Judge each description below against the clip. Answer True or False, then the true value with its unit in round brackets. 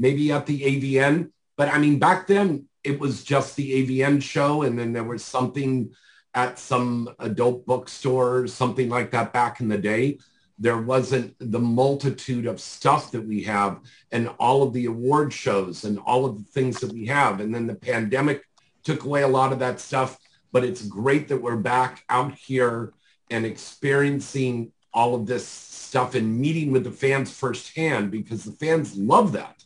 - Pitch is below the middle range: True (125 Hz)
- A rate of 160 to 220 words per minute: True (180 wpm)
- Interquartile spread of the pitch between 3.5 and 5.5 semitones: False (2.7 semitones)